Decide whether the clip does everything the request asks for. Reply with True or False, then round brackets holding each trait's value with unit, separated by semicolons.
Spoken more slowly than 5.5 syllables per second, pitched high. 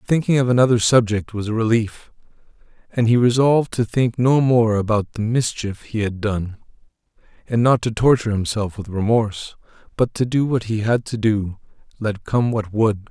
False (5.1 syllables/s; 115 Hz)